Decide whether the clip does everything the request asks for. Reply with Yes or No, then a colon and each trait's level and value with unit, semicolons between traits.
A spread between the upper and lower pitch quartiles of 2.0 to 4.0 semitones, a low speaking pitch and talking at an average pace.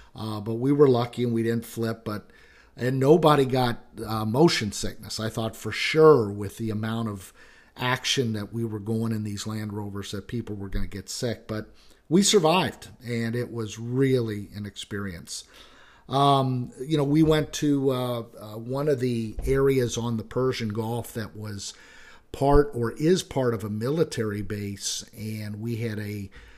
Yes: average, 3.3 semitones; low, 115 Hz; average, 180 wpm